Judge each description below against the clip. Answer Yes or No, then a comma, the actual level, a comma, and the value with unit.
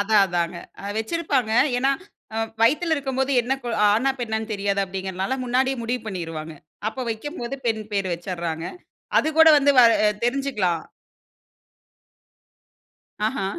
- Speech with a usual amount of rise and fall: No, wide, 5.7 semitones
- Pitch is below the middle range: No, high, 220 Hz